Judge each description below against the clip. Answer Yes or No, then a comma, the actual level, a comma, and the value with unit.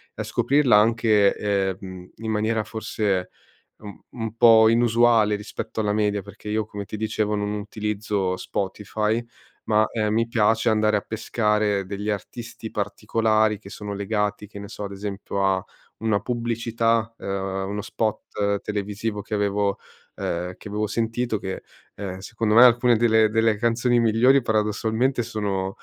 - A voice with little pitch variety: Yes, narrow, 1.9 semitones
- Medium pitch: No, low, 105 Hz